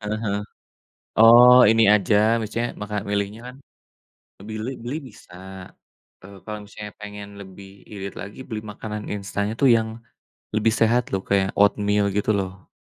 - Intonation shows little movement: Yes, narrow, 1.9 semitones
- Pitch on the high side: No, low, 105 Hz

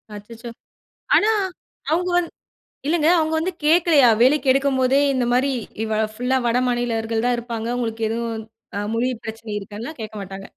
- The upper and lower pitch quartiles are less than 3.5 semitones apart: No, average, 3.9 semitones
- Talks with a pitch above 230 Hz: Yes, high, 245 Hz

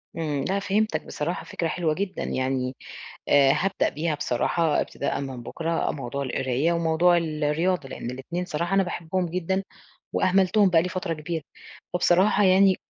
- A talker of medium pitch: Yes, medium, 165 Hz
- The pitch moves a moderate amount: Yes, average, 3.9 semitones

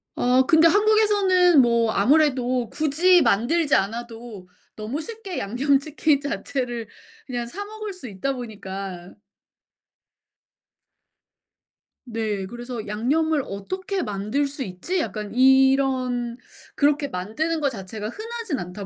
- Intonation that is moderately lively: No, wide, 6.3 semitones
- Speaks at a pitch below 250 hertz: No, very high, 260 Hz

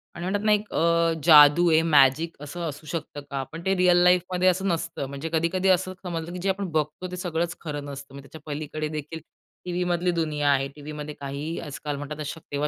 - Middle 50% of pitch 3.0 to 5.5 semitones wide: Yes, average, 3.3 semitones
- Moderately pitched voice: Yes, medium, 160 Hz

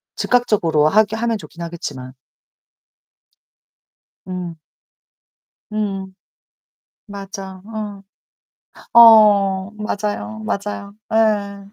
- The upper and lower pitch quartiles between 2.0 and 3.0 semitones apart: Yes, narrow, 2.5 semitones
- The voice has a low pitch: No, high, 200 Hz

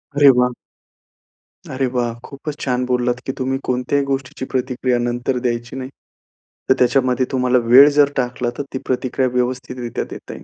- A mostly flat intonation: Yes, narrow, 1.3 semitones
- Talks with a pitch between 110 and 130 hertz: Yes, low, 125 Hz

